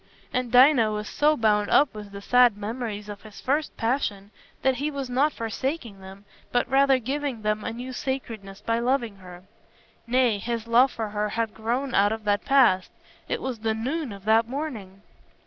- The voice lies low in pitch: No, high, 230 Hz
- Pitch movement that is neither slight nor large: Yes, average, 3.9 semitones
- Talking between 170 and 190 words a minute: Yes, average, 185 wpm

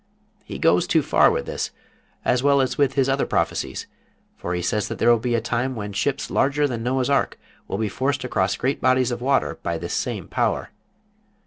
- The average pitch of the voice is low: Yes, low, 125 Hz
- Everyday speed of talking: No, fast, 210 wpm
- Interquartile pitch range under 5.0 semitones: Yes, average, 3.4 semitones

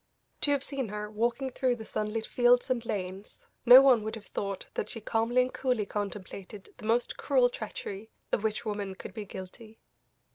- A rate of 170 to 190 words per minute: Yes, average, 185 wpm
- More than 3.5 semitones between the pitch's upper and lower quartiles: No, average, 3.0 semitones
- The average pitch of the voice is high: Yes, high, 220 Hz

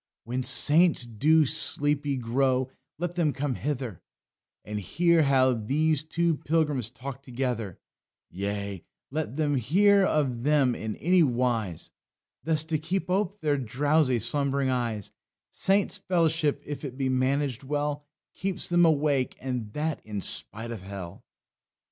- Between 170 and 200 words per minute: No, slow, 135 wpm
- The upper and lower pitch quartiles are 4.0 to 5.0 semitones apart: Yes, average, 4.3 semitones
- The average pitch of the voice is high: No, medium, 140 Hz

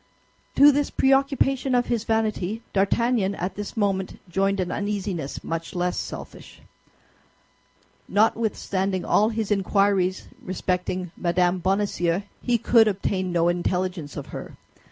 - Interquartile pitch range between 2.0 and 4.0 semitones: Yes, average, 3.5 semitones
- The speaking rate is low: Yes, slow, 120 wpm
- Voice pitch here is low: No, high, 195 Hz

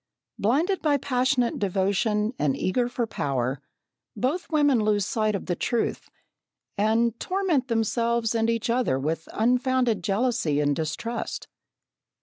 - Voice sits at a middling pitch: No, high, 230 Hz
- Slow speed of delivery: Yes, slow, 130 wpm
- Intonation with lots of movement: No, average, 4.2 semitones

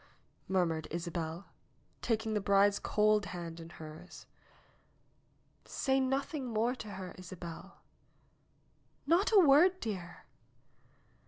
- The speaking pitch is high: Yes, high, 200 Hz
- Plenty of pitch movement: Yes, wide, 6.7 semitones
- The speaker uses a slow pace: Yes, slow, 100 wpm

